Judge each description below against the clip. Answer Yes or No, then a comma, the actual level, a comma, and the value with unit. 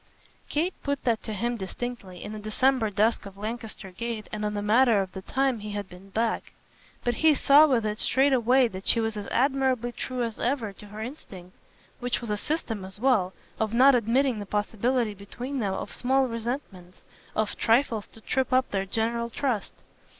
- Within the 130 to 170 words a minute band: No, average, 195 wpm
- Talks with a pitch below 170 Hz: No, high, 230 Hz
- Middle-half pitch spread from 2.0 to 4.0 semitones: Yes, average, 3.7 semitones